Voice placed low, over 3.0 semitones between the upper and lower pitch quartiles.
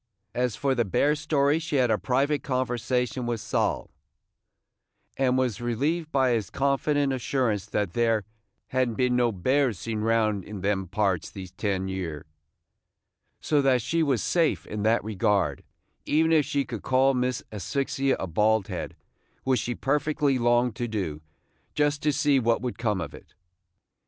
Yes: low, 125 Hz; average, 4.5 semitones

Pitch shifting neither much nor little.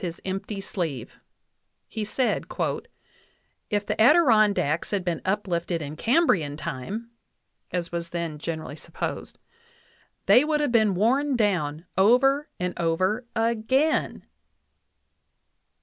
No: wide, 5.8 semitones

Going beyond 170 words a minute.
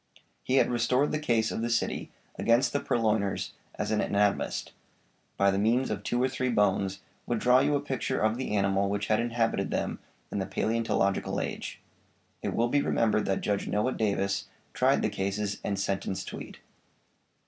Yes: average, 180 wpm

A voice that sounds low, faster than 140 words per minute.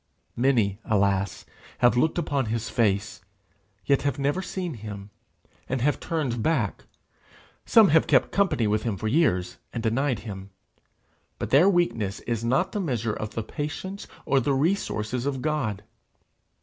Yes: low, 120 Hz; average, 150 wpm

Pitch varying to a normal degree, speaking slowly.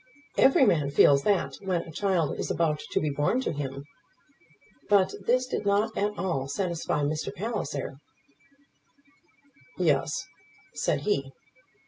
No: wide, 5.8 semitones; slow, 130 wpm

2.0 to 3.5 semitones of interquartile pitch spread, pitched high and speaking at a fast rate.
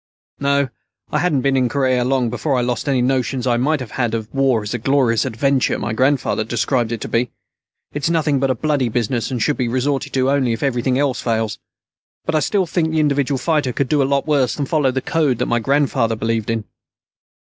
No: average, 2.9 semitones; low, 130 Hz; fast, 220 wpm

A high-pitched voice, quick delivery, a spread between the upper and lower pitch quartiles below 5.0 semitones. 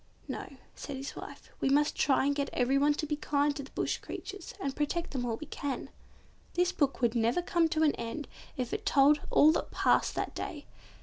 Yes: very high, 285 Hz; fast, 210 wpm; narrow, 2.4 semitones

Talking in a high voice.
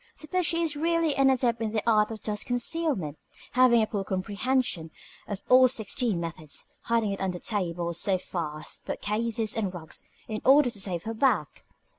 Yes: high, 220 Hz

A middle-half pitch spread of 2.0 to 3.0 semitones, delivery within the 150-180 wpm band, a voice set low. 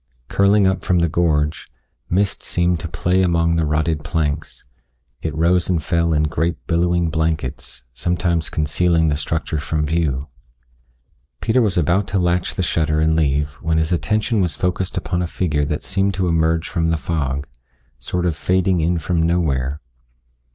Yes: narrow, 2.5 semitones; average, 165 wpm; very low, 85 Hz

